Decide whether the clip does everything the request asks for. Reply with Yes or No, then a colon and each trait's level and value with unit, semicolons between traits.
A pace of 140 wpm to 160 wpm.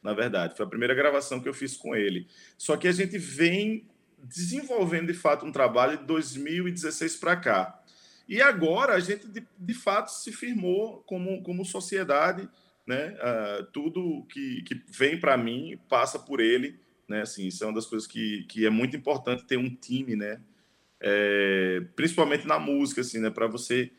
No: average, 180 wpm